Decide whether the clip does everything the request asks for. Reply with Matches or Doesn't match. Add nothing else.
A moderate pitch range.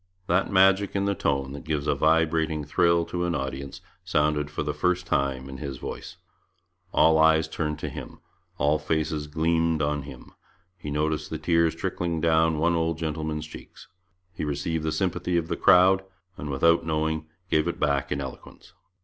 Doesn't match